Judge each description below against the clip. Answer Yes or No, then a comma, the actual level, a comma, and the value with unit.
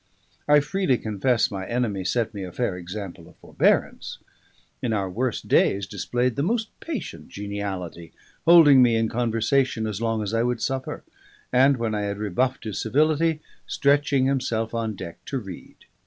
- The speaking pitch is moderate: No, low, 115 Hz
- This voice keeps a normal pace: Yes, average, 165 wpm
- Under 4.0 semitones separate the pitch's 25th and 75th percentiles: No, average, 4.7 semitones